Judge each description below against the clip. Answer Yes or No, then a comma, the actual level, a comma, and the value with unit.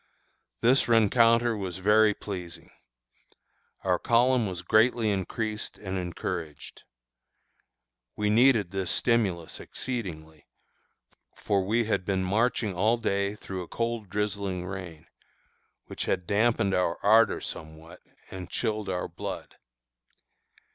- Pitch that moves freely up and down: No, average, 3.7 semitones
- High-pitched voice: No, low, 100 Hz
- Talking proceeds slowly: Yes, slow, 115 wpm